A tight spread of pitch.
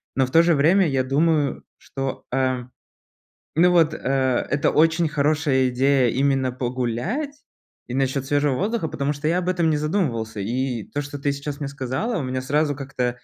No: average, 3.4 semitones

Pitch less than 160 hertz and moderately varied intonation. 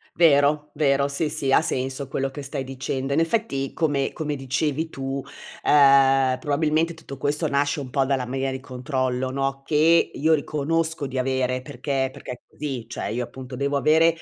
No: medium, 140 Hz; narrow, 2.2 semitones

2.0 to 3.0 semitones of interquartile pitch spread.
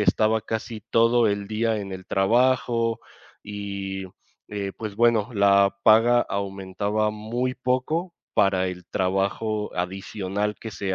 Yes: average, 2.7 semitones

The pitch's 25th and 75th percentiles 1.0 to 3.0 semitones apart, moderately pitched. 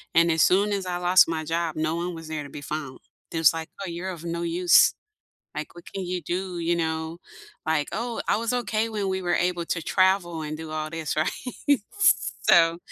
Yes: narrow, 2.6 semitones; medium, 170 Hz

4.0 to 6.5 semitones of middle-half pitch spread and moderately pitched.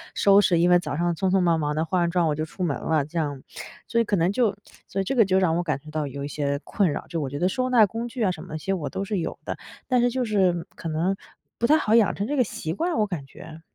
Yes: average, 4.9 semitones; medium, 180 Hz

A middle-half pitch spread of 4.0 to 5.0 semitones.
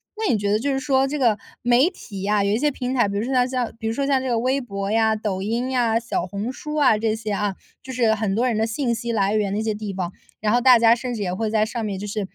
No: average, 3.4 semitones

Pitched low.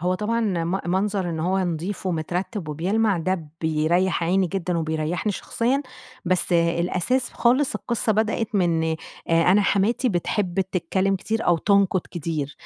No: medium, 185 Hz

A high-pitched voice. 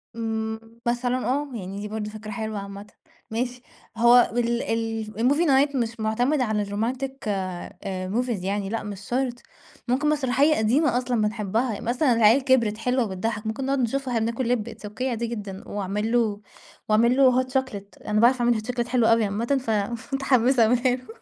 Yes: high, 230 Hz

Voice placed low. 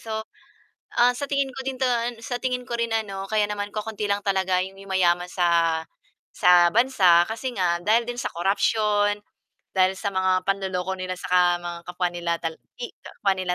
No: high, 195 Hz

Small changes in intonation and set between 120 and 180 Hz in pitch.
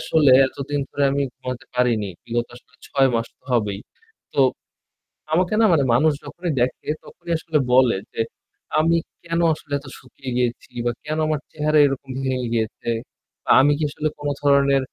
No: average, 3.6 semitones; medium, 140 Hz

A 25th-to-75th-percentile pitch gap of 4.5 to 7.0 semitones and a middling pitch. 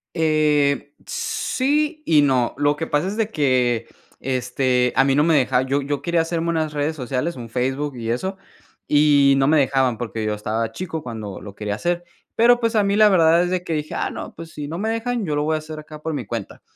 Yes: average, 4.8 semitones; medium, 150 Hz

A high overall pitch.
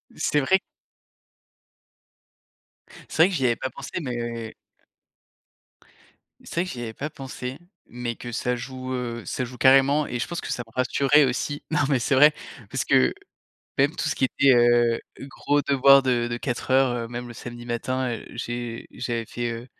No: low, 125 Hz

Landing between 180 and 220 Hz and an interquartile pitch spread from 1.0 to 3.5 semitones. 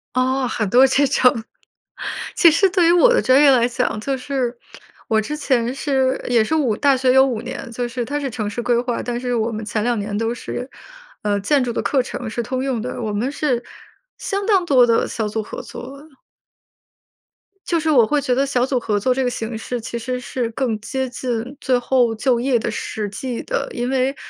No: very high, 250 Hz; narrow, 2.5 semitones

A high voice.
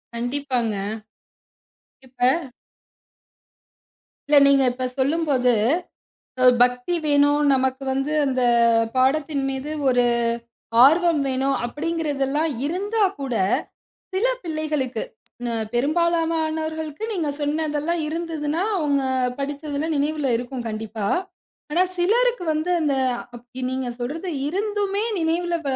Yes: very high, 290 Hz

